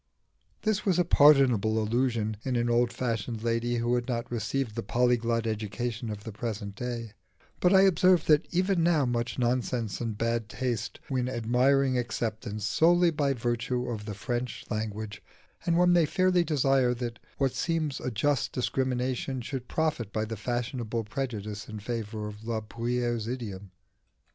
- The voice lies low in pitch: Yes, low, 120 Hz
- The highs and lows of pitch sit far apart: No, average, 3.2 semitones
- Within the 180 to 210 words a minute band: No, average, 160 wpm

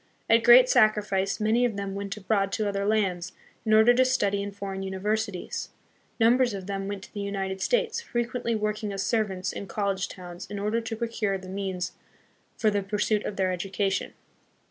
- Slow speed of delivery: No, average, 190 wpm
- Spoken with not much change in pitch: Yes, narrow, 2.2 semitones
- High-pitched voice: Yes, high, 205 Hz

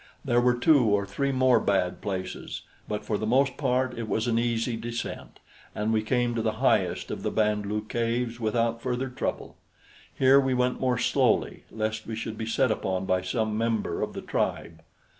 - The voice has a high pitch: No, low, 115 Hz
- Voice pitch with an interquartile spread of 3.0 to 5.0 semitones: No, narrow, 2.5 semitones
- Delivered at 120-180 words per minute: No, average, 195 wpm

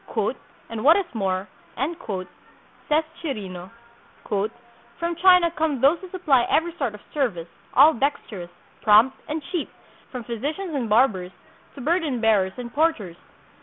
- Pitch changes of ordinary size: No, wide, 7.1 semitones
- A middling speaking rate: No, slow, 130 wpm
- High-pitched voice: Yes, very high, 255 Hz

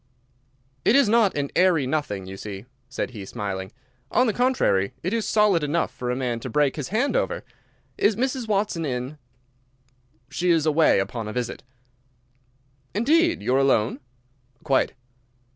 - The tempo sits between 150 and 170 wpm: Yes, average, 160 wpm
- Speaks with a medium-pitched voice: Yes, medium, 150 Hz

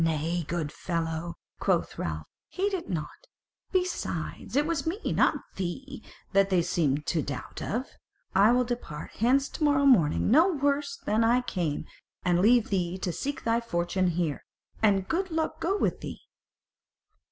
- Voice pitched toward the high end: Yes, high, 210 Hz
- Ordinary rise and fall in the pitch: No, wide, 8.4 semitones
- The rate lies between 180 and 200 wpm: No, average, 160 wpm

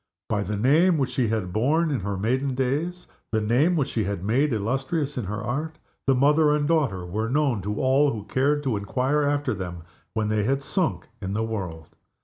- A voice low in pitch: Yes, low, 125 Hz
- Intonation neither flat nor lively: No, wide, 5.7 semitones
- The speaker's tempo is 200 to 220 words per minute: Yes, fast, 205 wpm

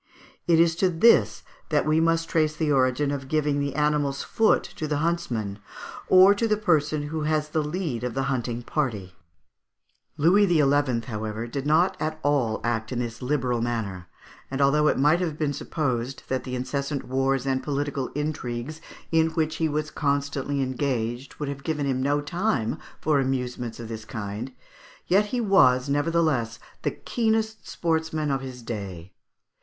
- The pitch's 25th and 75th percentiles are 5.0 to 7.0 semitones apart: No, average, 4.0 semitones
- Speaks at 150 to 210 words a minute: Yes, average, 170 wpm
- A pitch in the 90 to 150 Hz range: Yes, medium, 140 Hz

